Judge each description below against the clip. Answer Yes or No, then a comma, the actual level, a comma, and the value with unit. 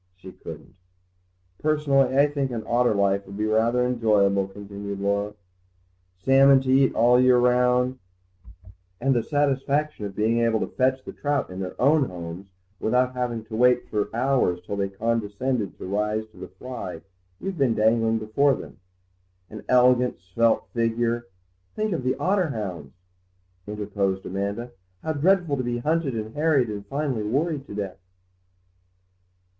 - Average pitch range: Yes, average, 4.5 semitones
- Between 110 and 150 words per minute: No, average, 160 wpm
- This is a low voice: Yes, low, 120 Hz